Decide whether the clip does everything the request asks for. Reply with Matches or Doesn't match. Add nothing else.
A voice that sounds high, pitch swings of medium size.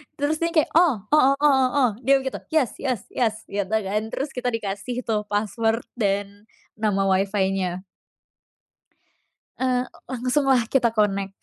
Matches